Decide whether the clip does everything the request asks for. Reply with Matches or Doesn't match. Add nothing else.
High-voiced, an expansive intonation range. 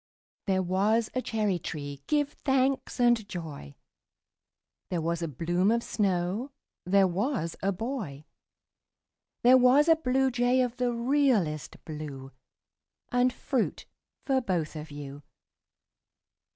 Matches